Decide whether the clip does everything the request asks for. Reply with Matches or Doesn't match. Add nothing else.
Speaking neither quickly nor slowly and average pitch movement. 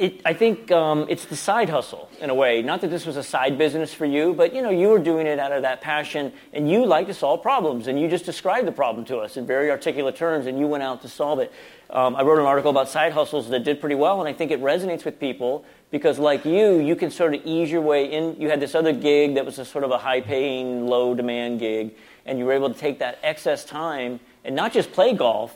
Doesn't match